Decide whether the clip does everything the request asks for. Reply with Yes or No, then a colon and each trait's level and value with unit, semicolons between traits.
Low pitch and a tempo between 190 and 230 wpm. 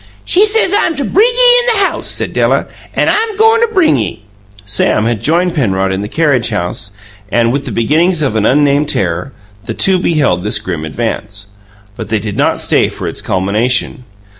Yes: low, 130 Hz; average, 195 wpm